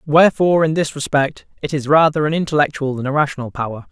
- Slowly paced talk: No, average, 200 wpm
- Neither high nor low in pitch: Yes, medium, 145 Hz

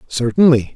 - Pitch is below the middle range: Yes, low, 130 Hz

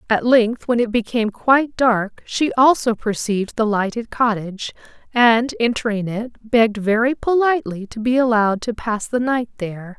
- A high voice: Yes, high, 230 Hz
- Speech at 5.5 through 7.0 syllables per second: No, 5.0 syllables/s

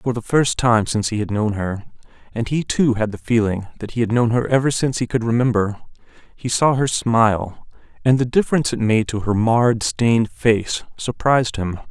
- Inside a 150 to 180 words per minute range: No, average, 195 wpm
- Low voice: Yes, low, 115 Hz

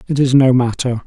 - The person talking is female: No, male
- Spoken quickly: Yes, fast, 225 wpm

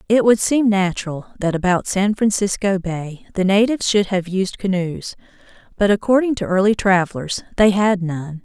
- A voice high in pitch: Yes, high, 195 Hz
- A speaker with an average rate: Yes, average, 165 wpm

